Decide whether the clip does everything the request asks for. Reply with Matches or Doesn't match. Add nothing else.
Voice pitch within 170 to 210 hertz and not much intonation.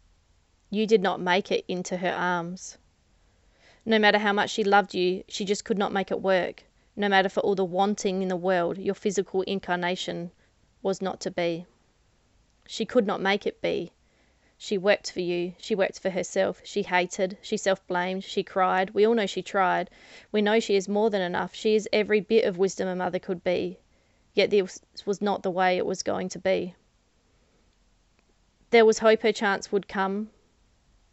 Matches